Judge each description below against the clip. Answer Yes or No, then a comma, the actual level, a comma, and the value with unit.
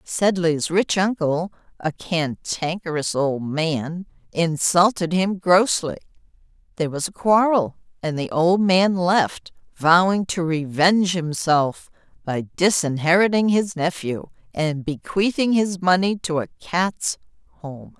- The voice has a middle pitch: Yes, medium, 175 Hz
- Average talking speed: No, slow, 115 wpm